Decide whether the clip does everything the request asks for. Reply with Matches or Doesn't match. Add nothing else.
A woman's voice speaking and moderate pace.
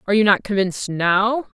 Matches